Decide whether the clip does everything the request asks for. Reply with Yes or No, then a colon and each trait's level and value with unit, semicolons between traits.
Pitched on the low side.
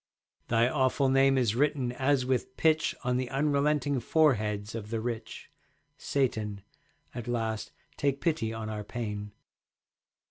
Yes: low, 125 Hz